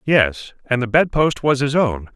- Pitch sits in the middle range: No, low, 130 Hz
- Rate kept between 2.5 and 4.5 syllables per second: Yes, 4.2 syllables/s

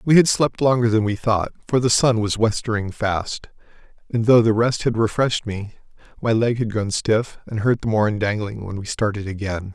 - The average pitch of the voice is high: No, low, 110 Hz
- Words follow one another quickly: Yes, fast, 215 wpm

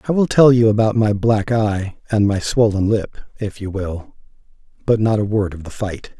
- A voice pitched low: Yes, low, 105 Hz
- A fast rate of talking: Yes, fast, 215 wpm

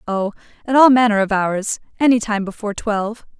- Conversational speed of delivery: Yes, average, 160 wpm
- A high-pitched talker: Yes, high, 220 Hz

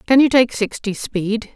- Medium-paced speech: Yes, average, 195 wpm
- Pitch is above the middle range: Yes, high, 225 Hz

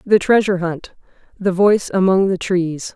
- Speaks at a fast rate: No, average, 140 wpm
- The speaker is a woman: Yes, female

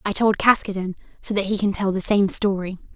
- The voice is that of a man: No, female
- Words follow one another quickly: Yes, fast, 225 wpm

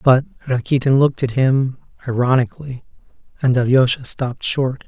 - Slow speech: Yes, slow, 125 wpm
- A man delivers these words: Yes, male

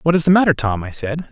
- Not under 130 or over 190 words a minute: No, fast, 320 wpm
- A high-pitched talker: No, medium, 145 Hz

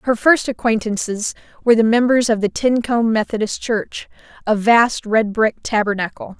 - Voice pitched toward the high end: Yes, high, 225 Hz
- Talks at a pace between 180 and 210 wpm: No, average, 150 wpm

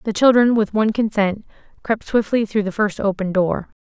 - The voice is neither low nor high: No, high, 210 Hz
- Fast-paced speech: No, average, 190 wpm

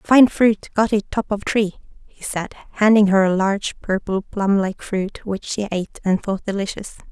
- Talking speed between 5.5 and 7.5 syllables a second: No, 4.7 syllables/s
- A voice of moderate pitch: No, high, 200 Hz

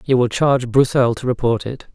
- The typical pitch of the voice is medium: No, low, 125 Hz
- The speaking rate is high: Yes, fast, 215 wpm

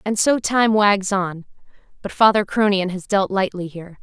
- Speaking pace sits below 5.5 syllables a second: Yes, 4.8 syllables/s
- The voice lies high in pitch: Yes, high, 200 Hz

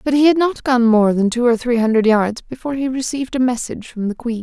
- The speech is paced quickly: Yes, fast, 270 wpm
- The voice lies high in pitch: Yes, high, 245 Hz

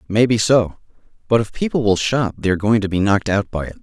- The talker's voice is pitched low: Yes, low, 110 Hz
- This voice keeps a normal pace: No, fast, 235 wpm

